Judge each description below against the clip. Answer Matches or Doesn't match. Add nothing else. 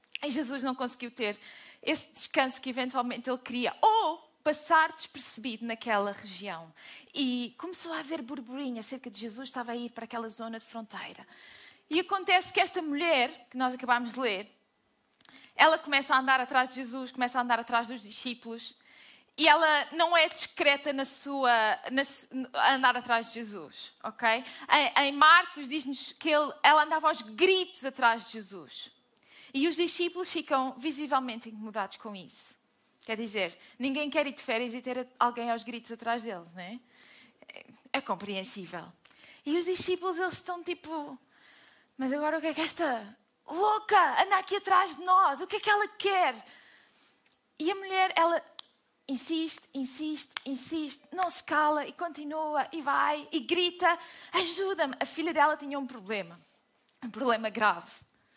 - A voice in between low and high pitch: Doesn't match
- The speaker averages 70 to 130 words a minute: Doesn't match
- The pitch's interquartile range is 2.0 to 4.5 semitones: Doesn't match